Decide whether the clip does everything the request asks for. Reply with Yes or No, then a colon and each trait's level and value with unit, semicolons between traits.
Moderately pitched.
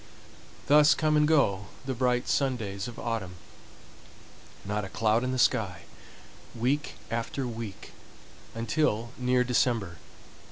No: low, 120 Hz